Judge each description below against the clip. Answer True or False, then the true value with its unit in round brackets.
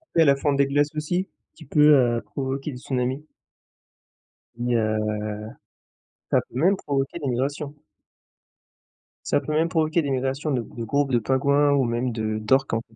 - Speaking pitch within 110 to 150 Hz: True (140 Hz)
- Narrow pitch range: False (3.1 semitones)